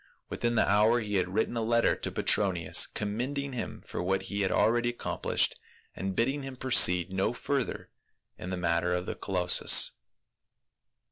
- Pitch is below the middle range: Yes, low, 105 Hz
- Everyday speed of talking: Yes, average, 160 wpm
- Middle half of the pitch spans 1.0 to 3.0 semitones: No, average, 4.6 semitones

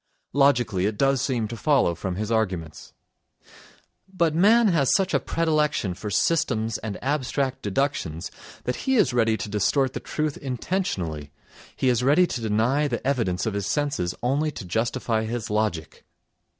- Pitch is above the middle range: No, low, 120 Hz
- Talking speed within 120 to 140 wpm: No, average, 160 wpm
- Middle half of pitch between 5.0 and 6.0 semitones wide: Yes, wide, 5.5 semitones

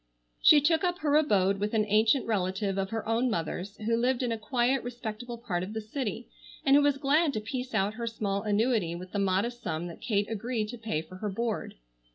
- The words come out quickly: Yes, fast, 220 wpm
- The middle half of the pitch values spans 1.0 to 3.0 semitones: No, average, 3.8 semitones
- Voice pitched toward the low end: No, high, 220 Hz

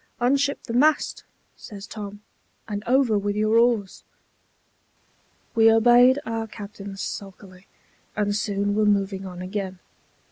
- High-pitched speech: Yes, high, 210 Hz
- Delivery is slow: Yes, slow, 120 wpm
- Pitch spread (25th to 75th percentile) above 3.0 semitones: No, narrow, 2.5 semitones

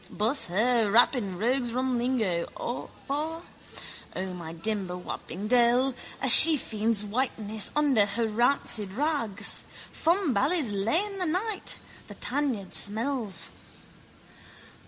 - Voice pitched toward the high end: Yes, high, 235 Hz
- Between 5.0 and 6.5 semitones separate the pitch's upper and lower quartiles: Yes, wide, 5.4 semitones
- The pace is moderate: No, slow, 110 wpm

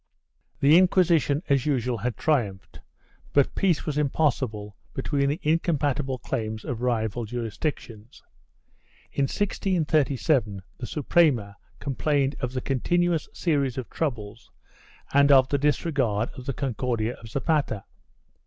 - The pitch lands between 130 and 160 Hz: Yes, low, 135 Hz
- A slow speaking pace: Yes, slow, 125 wpm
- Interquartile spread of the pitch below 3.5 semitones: No, average, 4.3 semitones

